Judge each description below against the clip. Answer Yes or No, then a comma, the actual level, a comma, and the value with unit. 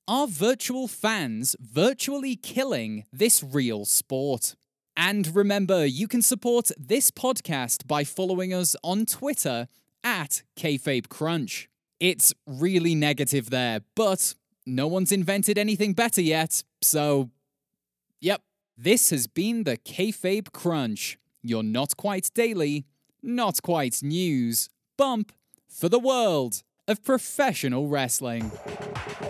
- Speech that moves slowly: Yes, slow, 115 wpm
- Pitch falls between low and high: Yes, medium, 170 Hz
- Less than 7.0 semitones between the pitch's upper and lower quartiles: No, wide, 7.7 semitones